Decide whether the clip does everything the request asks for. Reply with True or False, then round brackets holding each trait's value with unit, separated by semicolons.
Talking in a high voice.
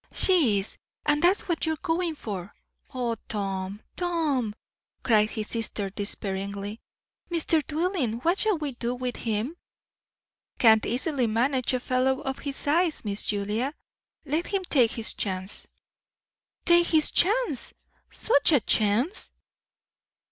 True (255 Hz)